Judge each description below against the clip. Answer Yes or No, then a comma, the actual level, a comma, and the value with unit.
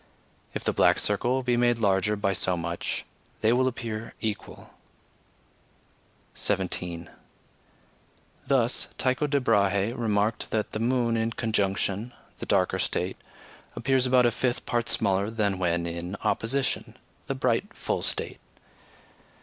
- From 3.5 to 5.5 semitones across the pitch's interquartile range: Yes, average, 3.8 semitones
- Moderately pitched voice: No, low, 110 Hz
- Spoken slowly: Yes, slow, 130 wpm